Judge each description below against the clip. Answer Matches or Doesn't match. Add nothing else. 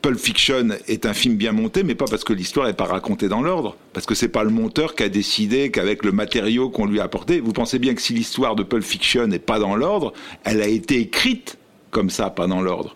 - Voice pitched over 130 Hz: Doesn't match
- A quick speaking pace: Matches